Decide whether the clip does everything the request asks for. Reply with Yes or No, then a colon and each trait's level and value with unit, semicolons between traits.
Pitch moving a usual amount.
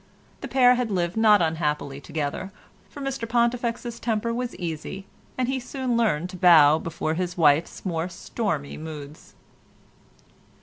No: wide, 6.8 semitones